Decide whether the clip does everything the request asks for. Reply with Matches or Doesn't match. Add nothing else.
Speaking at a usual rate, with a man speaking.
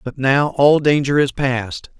Matches